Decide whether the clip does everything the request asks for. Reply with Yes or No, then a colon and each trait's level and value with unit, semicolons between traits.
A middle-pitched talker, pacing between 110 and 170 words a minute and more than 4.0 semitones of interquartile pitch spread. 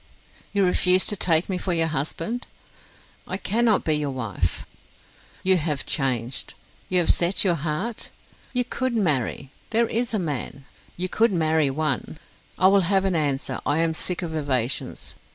Yes: medium, 165 Hz; average, 165 wpm; average, 4.8 semitones